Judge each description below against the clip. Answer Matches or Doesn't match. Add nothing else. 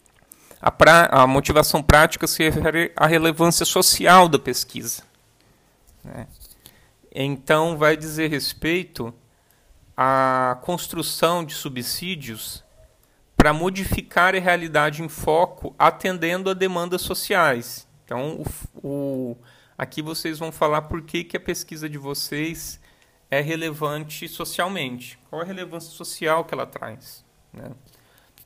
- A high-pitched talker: Doesn't match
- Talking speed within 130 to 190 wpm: Doesn't match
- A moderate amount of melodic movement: Matches